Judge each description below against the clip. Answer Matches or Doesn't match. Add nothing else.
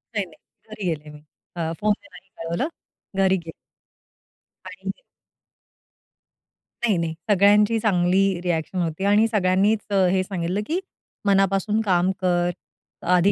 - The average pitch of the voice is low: Doesn't match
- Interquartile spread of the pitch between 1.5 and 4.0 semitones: Matches